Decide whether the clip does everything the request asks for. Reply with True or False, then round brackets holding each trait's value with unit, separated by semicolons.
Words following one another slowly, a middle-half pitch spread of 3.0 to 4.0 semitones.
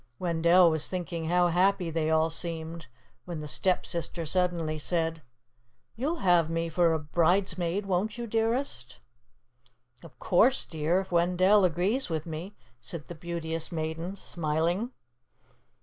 False (130 wpm; 2.4 semitones)